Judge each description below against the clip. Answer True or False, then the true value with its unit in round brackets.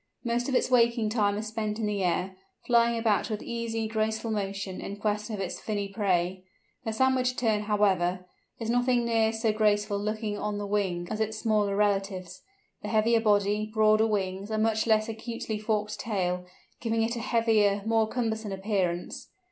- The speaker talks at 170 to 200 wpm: True (175 wpm)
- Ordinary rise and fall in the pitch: False (1.9 semitones)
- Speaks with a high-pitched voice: True (215 Hz)